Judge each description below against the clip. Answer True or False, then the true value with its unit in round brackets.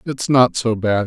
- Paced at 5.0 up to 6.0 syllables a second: False (4.1 syllables/s)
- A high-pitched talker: False (120 Hz)